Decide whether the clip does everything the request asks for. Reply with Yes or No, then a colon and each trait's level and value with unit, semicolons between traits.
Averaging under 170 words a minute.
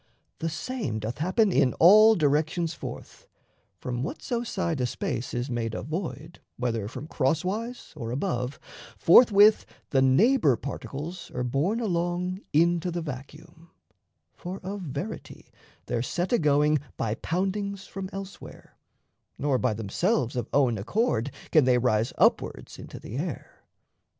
Yes: average, 140 wpm